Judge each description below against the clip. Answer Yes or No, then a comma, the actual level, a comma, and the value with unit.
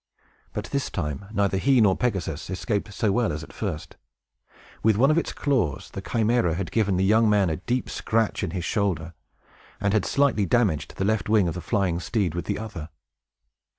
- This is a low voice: Yes, low, 100 Hz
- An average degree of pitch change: Yes, average, 4.1 semitones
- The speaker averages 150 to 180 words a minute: No, average, 195 wpm